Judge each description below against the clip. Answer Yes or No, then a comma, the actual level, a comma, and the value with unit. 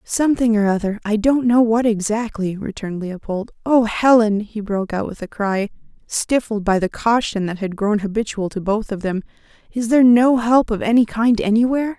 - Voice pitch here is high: Yes, high, 220 Hz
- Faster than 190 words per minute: No, average, 180 wpm